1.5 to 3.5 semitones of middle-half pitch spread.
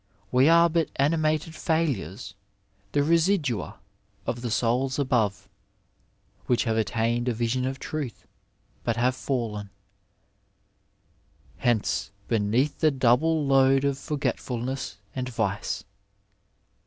No: average, 4.1 semitones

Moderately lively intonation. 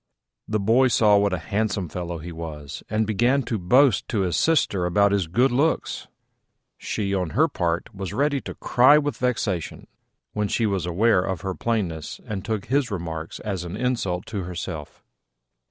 Yes: average, 5.0 semitones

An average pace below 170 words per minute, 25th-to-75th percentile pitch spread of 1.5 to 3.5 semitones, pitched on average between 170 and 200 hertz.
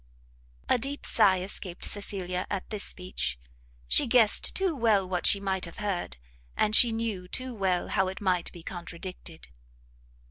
Yes: average, 155 wpm; average, 3.1 semitones; high, 190 Hz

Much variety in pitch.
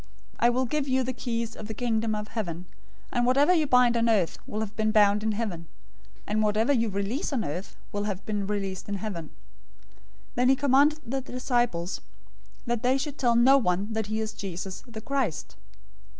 No: average, 3.6 semitones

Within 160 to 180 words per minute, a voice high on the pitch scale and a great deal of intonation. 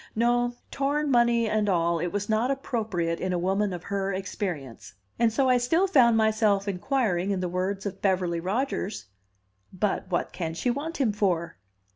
No: average, 175 wpm; high, 205 Hz; average, 4.7 semitones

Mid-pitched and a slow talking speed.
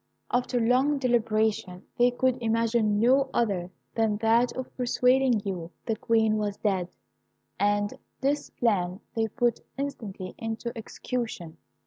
No: high, 225 Hz; slow, 125 wpm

